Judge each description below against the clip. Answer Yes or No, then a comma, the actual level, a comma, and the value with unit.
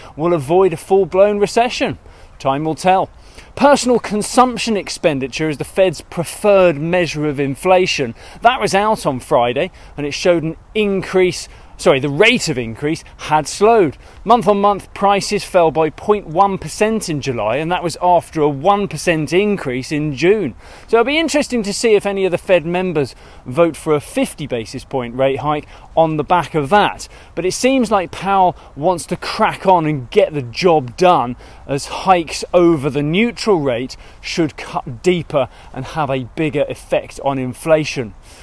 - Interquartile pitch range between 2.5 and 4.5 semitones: No, average, 5.3 semitones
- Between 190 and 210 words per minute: No, average, 170 wpm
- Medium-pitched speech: Yes, medium, 170 Hz